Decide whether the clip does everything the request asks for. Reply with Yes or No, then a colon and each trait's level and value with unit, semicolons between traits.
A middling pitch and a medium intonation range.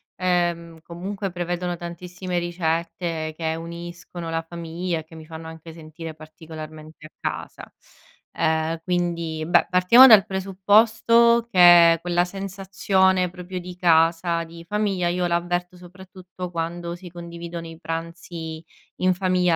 No: medium, 175 Hz; narrow, 1.8 semitones